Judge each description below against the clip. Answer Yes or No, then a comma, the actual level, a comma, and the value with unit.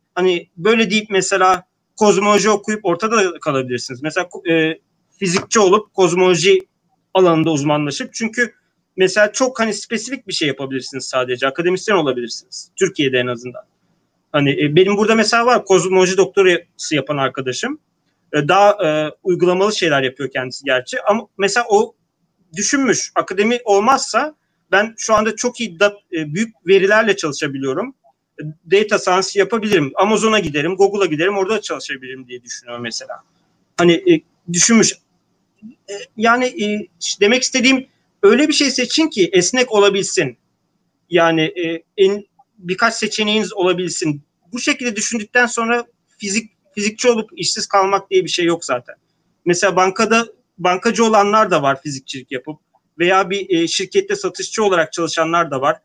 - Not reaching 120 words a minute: No, average, 135 wpm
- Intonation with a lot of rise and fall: No, average, 4.5 semitones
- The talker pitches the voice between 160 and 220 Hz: Yes, high, 190 Hz